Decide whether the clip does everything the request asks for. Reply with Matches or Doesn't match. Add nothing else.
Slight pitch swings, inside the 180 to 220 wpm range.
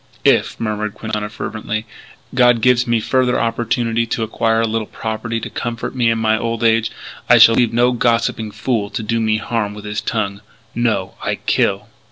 Matches